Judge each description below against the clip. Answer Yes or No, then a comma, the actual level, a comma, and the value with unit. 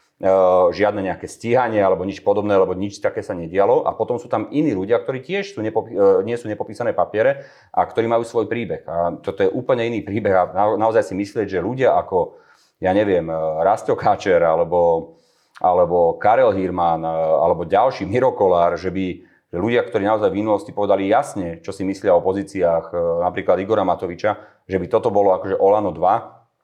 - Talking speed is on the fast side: Yes, fast, 175 wpm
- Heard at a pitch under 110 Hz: Yes, low, 100 Hz